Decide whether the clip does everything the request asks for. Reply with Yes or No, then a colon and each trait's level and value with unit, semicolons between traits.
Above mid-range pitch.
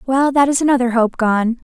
Yes: very high, 250 Hz